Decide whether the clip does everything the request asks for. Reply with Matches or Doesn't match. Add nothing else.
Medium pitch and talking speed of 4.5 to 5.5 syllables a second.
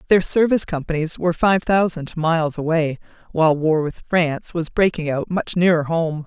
Matches